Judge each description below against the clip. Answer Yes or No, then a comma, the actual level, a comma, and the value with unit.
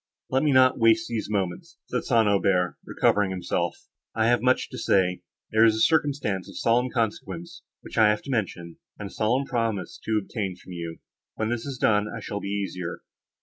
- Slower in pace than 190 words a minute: No, average, 195 wpm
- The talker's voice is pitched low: Yes, low, 110 Hz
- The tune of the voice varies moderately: Yes, average, 3.9 semitones